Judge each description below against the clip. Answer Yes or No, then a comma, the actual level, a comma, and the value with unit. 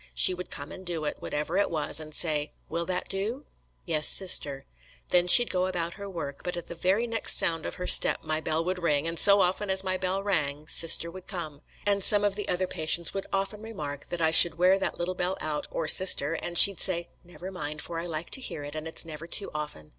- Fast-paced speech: Yes, fast, 240 wpm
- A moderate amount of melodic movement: Yes, average, 3.3 semitones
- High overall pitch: No, medium, 175 Hz